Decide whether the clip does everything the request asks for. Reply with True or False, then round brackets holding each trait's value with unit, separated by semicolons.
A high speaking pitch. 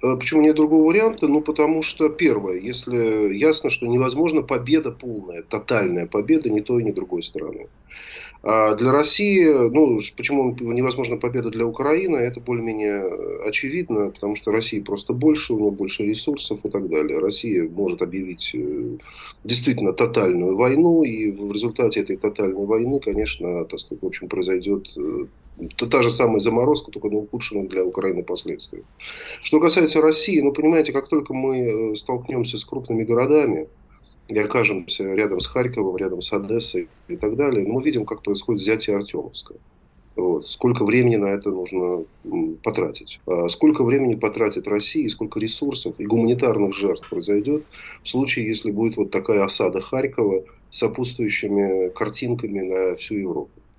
False (120 Hz)